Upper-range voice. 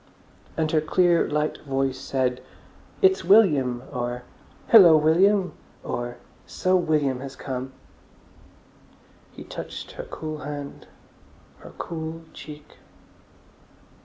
No: medium, 150 Hz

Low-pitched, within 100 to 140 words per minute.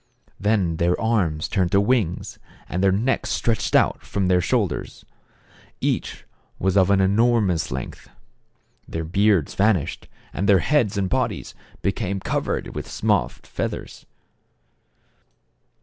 Yes: very low, 95 Hz; slow, 135 wpm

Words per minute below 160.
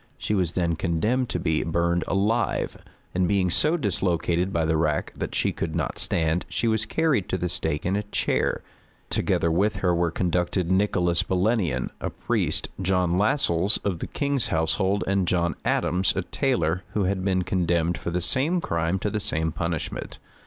No: average, 180 wpm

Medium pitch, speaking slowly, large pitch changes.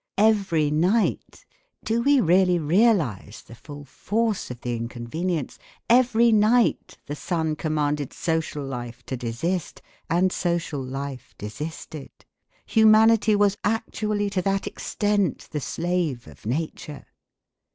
Yes: medium, 170 Hz; slow, 120 wpm; wide, 6.6 semitones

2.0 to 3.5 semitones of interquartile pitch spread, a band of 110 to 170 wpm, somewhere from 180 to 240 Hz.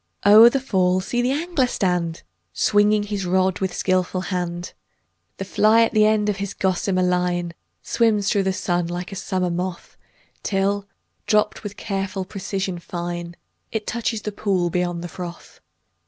Yes: average, 2.8 semitones; average, 165 wpm; high, 190 Hz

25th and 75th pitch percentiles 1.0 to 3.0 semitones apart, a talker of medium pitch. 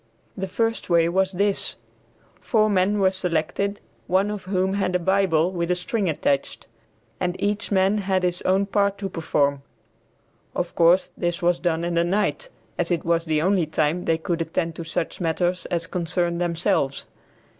Yes: narrow, 2.6 semitones; medium, 180 Hz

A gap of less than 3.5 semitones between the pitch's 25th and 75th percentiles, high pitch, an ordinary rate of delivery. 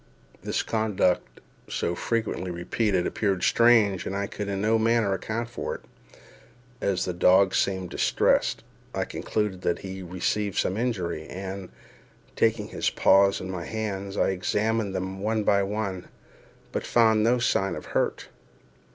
No: average, 2.7 semitones; low, 100 Hz; average, 155 wpm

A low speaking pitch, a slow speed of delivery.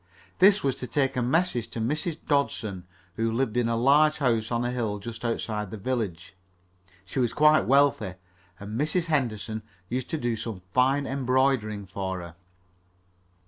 No: low, 120 Hz; average, 165 wpm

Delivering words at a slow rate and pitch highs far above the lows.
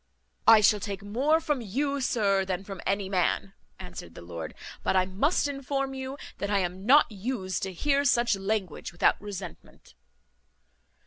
No: average, 165 wpm; wide, 5.8 semitones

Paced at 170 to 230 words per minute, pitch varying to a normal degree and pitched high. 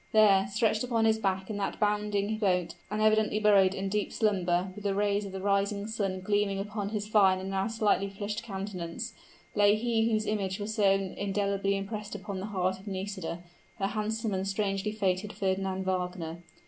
No: average, 185 wpm; narrow, 1.7 semitones; high, 200 Hz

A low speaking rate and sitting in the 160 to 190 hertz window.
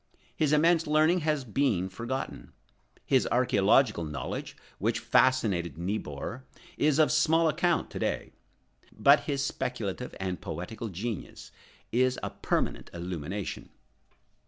No: slow, 115 wpm; low, 125 Hz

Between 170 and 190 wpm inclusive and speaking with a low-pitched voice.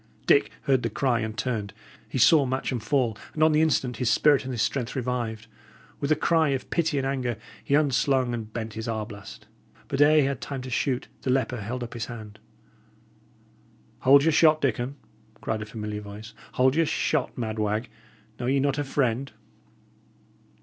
Yes: average, 185 wpm; low, 125 Hz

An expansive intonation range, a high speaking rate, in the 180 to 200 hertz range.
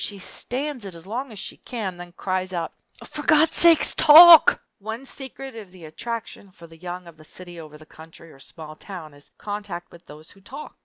Yes: wide, 6.2 semitones; fast, 210 wpm; medium, 185 Hz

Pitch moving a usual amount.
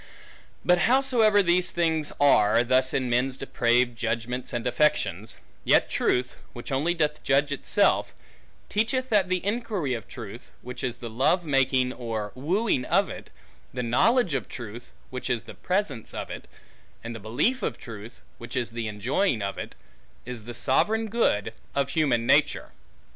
No: wide, 6.8 semitones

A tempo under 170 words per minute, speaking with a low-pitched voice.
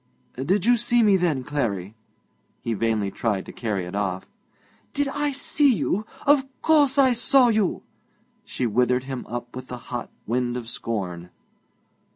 Yes: average, 160 wpm; low, 130 Hz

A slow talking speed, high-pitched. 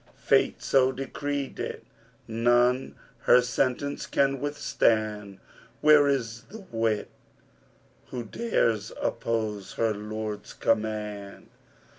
No: slow, 100 wpm; low, 115 Hz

